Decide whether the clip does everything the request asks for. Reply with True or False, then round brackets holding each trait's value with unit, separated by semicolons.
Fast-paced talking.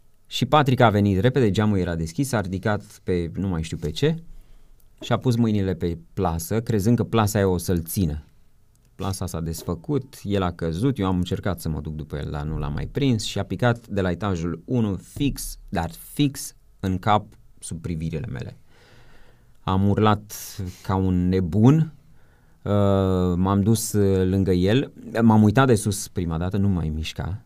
True (180 wpm)